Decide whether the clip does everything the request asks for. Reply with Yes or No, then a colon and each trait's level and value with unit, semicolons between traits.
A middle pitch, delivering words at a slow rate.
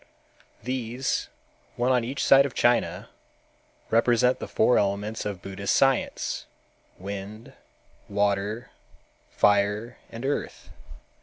No: low, 115 Hz; slow, 100 wpm